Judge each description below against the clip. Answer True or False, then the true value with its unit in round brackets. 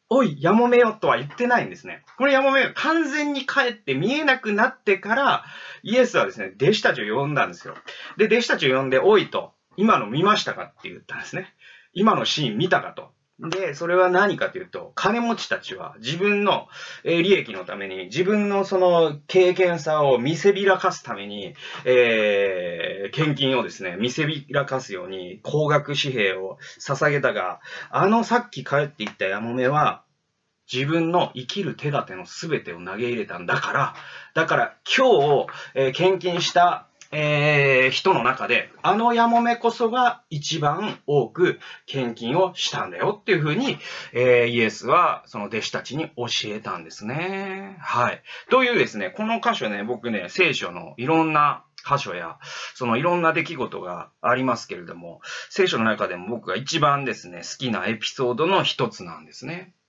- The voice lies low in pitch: False (165 Hz)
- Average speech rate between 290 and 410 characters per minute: True (340 characters per minute)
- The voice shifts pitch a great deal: True (8.4 semitones)